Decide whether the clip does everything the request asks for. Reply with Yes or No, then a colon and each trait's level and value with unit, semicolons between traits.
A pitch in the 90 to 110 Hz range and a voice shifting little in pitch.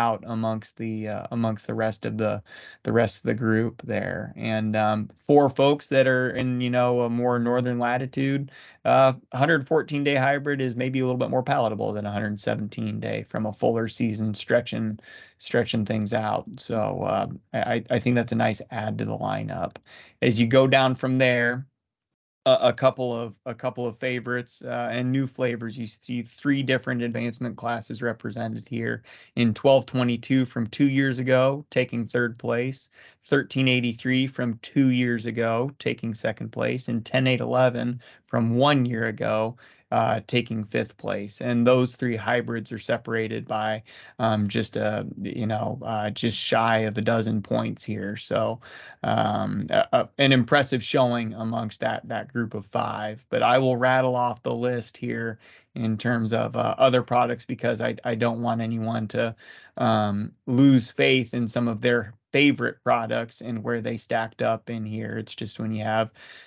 No: low, 120 Hz; narrow, 2.3 semitones